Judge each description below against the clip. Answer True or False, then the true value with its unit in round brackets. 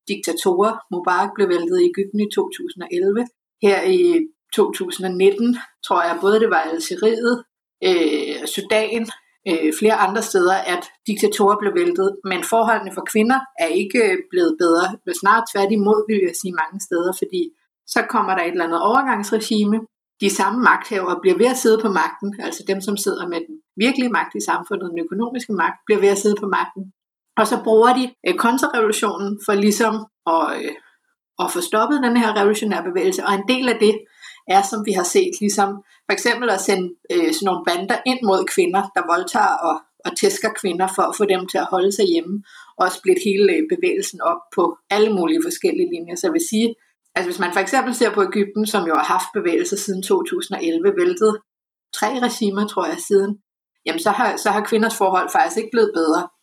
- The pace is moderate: True (190 wpm)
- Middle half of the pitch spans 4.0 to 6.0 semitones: True (4.7 semitones)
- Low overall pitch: False (215 Hz)